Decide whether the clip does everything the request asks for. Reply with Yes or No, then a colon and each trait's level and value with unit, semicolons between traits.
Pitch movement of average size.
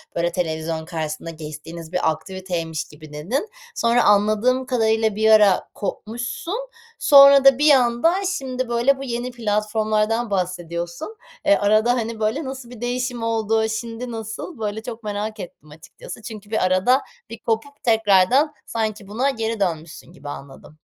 Yes: average, 5.0 semitones